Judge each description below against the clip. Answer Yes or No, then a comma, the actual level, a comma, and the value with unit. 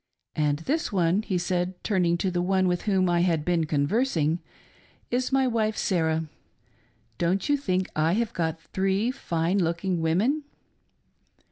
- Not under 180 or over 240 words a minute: No, average, 150 wpm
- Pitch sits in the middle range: Yes, medium, 180 Hz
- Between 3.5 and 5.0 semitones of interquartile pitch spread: Yes, average, 3.9 semitones